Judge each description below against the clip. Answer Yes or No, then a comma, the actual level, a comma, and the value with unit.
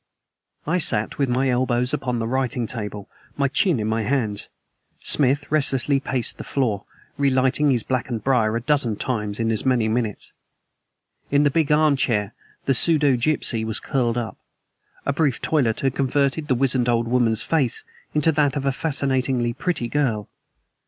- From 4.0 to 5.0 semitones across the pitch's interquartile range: No, average, 3.4 semitones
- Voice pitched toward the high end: No, low, 130 Hz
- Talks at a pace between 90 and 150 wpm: No, average, 165 wpm